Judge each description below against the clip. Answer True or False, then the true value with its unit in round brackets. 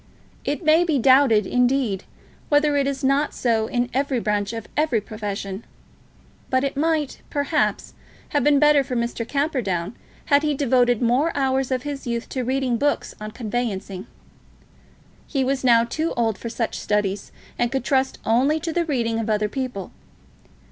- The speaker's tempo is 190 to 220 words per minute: False (165 wpm)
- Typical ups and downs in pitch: True (3.9 semitones)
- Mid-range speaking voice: False (255 Hz)